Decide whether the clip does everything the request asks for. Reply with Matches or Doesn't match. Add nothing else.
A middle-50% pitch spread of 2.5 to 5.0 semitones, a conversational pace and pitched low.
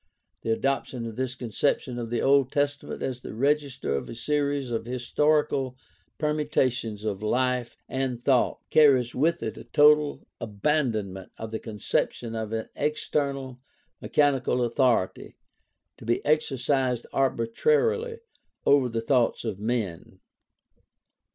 Doesn't match